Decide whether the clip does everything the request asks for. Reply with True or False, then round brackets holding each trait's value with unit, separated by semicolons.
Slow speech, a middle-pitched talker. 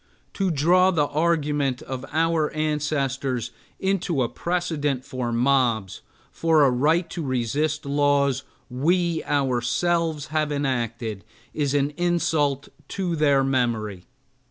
True (115 wpm; 145 Hz)